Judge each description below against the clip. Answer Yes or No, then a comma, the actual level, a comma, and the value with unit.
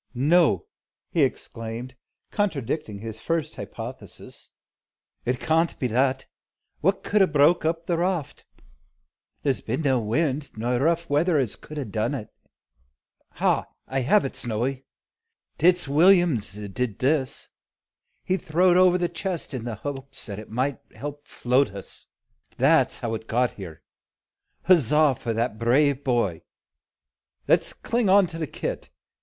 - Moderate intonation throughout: No, wide, 5.7 semitones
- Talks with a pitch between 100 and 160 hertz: Yes, medium, 140 Hz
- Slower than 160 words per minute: Yes, average, 145 wpm